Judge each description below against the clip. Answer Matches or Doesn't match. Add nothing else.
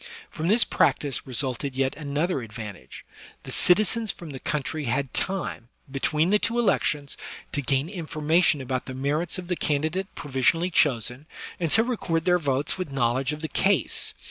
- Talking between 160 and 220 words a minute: Matches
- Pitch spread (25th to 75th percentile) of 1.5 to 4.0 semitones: Doesn't match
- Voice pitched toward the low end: Doesn't match